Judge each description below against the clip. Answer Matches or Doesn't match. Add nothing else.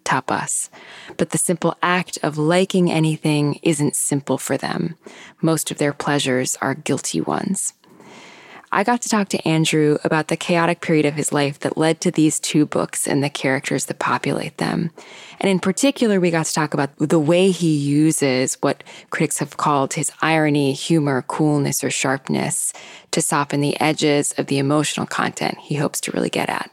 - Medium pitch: Matches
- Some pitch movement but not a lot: Matches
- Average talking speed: Matches